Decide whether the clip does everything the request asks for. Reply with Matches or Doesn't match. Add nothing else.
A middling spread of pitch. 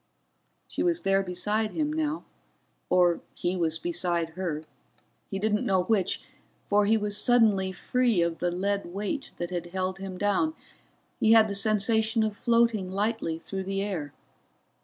Matches